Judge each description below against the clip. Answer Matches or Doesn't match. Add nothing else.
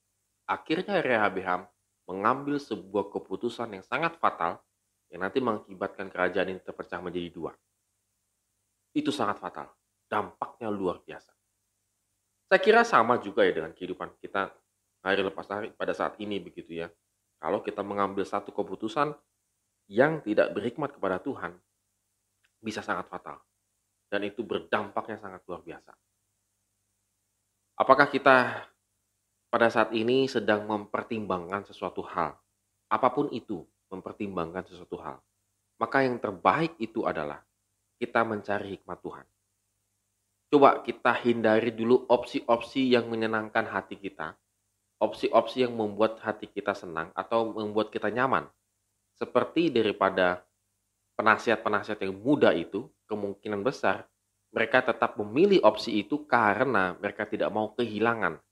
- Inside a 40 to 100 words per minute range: Doesn't match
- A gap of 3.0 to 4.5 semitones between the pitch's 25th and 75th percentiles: Doesn't match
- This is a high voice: Doesn't match